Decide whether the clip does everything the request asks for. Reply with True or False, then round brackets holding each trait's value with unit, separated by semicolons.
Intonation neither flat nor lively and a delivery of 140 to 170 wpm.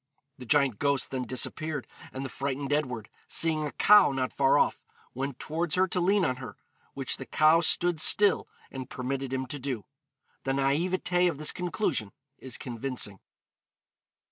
True (3.9 semitones; 165 wpm)